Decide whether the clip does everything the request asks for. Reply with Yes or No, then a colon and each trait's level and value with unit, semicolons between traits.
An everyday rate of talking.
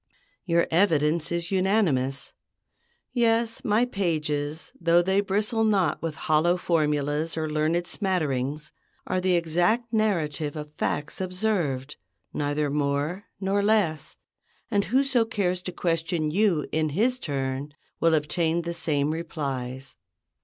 No: slow, 125 wpm